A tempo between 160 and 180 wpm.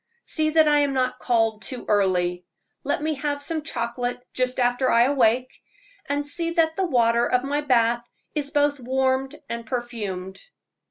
Yes: average, 165 wpm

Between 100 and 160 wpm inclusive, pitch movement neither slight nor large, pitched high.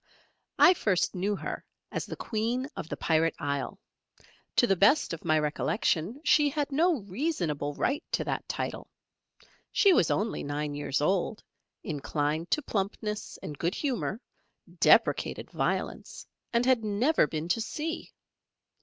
No: average, 145 wpm; wide, 8.6 semitones; high, 200 Hz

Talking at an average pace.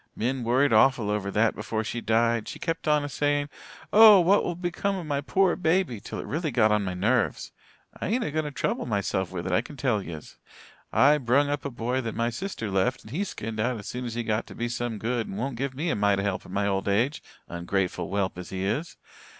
No: fast, 250 wpm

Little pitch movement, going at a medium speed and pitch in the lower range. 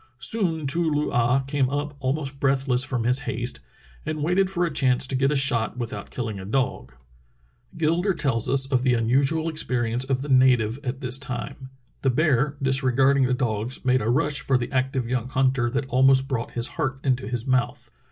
Yes: narrow, 2.2 semitones; average, 195 wpm; low, 130 Hz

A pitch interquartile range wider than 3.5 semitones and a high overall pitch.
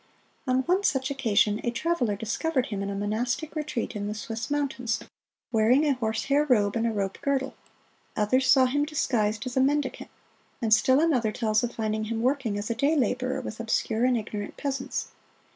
Yes: average, 3.9 semitones; high, 240 Hz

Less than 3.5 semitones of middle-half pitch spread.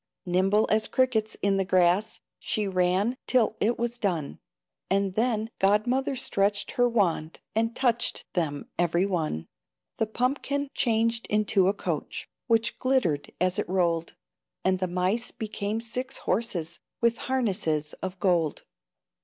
No: average, 4.2 semitones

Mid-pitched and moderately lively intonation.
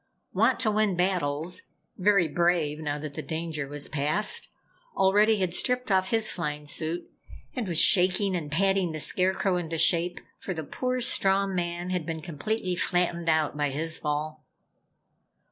Yes: medium, 175 Hz; average, 3.6 semitones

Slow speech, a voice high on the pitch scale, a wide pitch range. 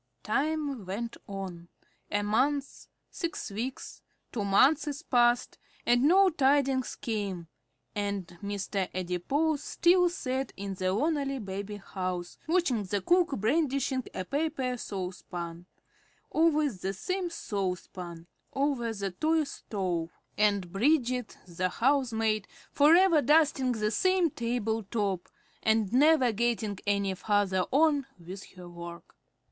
Yes: slow, 120 wpm; high, 225 Hz; wide, 6.6 semitones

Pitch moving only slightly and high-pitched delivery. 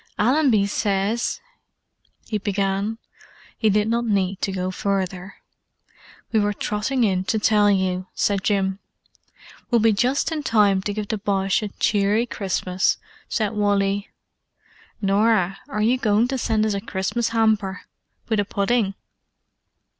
Yes: narrow, 2.3 semitones; high, 205 Hz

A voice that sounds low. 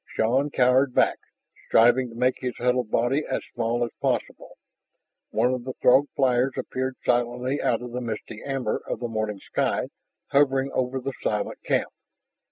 Yes: low, 125 Hz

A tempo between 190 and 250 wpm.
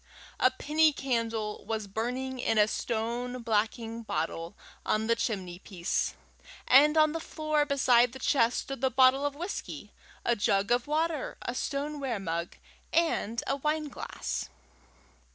No: average, 140 wpm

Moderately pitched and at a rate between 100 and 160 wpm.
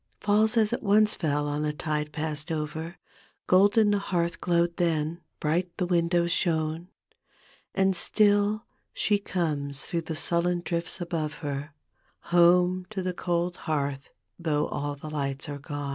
Yes: medium, 170 Hz; average, 150 wpm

